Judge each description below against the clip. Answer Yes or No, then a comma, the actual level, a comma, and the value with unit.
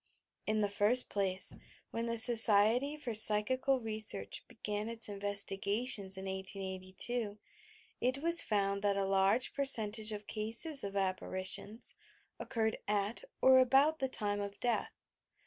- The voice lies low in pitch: No, high, 215 Hz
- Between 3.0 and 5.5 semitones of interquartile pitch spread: Yes, average, 3.4 semitones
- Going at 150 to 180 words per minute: No, slow, 135 wpm